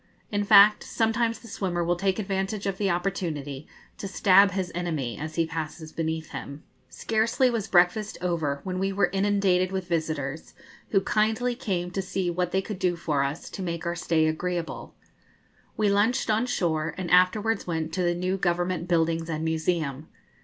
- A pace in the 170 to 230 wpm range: Yes, average, 175 wpm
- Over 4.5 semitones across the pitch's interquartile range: No, average, 3.4 semitones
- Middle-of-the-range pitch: Yes, medium, 180 Hz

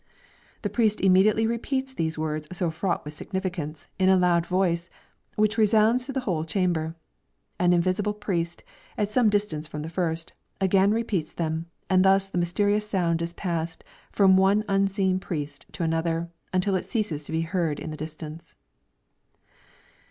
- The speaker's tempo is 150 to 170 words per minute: Yes, average, 160 wpm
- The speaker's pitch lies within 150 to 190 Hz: Yes, medium, 185 Hz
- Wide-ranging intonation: No, average, 3.8 semitones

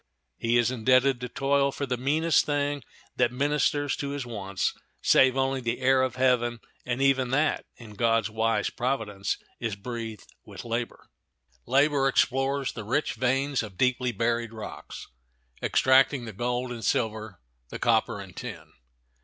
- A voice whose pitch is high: No, low, 125 Hz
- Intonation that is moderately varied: Yes, average, 3.0 semitones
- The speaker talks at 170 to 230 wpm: No, average, 155 wpm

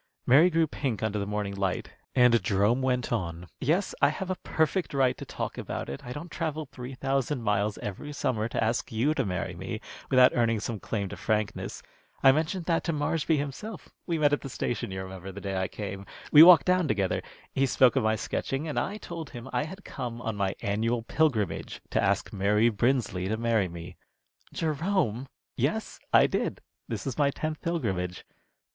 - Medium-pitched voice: No, low, 125 Hz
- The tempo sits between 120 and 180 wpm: No, average, 195 wpm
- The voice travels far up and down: Yes, wide, 6.4 semitones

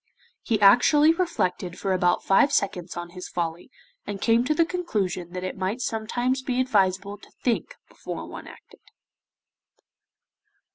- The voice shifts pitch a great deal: Yes, wide, 5.7 semitones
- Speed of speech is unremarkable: Yes, average, 145 wpm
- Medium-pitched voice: No, high, 205 Hz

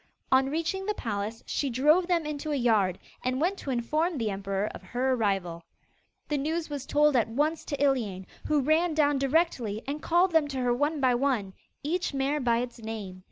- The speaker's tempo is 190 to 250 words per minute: Yes, average, 200 wpm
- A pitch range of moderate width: Yes, average, 5.0 semitones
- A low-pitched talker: No, very high, 270 Hz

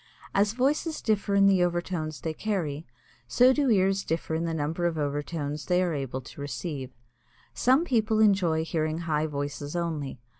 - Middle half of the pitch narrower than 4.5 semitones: No, average, 5.0 semitones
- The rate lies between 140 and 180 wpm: Yes, average, 165 wpm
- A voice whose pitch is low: No, medium, 170 Hz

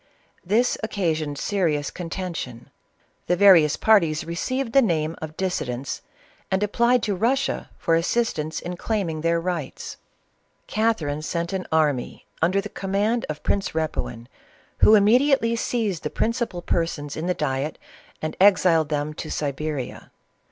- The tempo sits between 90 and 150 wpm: Yes, slow, 135 wpm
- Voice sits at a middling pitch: Yes, medium, 175 Hz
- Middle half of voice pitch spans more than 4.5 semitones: Yes, average, 5.2 semitones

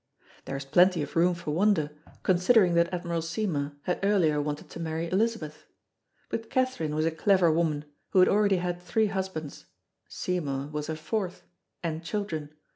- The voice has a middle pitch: Yes, medium, 170 Hz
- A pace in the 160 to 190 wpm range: Yes, average, 165 wpm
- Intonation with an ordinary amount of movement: Yes, average, 3.5 semitones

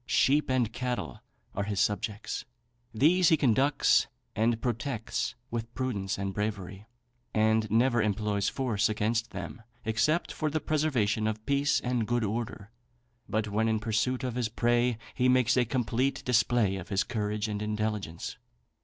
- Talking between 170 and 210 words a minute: No, average, 150 wpm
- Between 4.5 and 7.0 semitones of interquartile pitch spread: No, average, 3.1 semitones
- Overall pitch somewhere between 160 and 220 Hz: No, low, 115 Hz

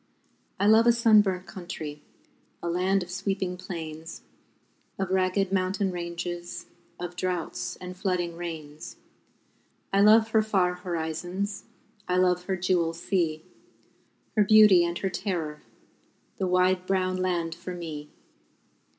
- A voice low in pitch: No, medium, 180 Hz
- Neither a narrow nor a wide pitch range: No, narrow, 2.0 semitones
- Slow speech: Yes, slow, 125 wpm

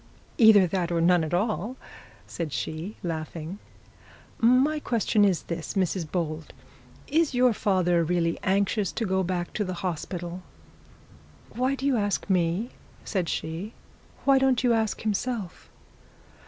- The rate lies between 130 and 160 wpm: Yes, average, 140 wpm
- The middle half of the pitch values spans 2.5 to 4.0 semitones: No, average, 4.8 semitones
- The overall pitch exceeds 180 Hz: Yes, high, 190 Hz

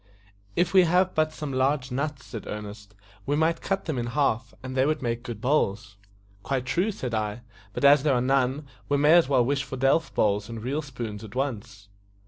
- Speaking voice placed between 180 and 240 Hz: No, low, 130 Hz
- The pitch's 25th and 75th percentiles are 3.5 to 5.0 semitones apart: Yes, average, 4.2 semitones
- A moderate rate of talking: No, fast, 210 wpm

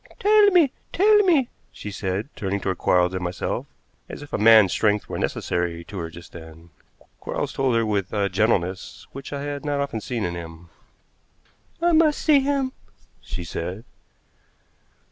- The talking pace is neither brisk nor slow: Yes, average, 165 wpm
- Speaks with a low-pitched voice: Yes, low, 105 Hz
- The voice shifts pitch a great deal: Yes, wide, 8.7 semitones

